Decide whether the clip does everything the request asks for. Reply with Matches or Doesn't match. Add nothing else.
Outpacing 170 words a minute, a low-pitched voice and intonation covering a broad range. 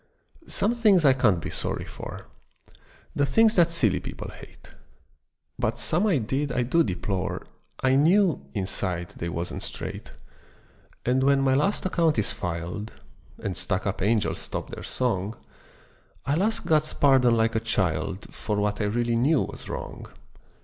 Doesn't match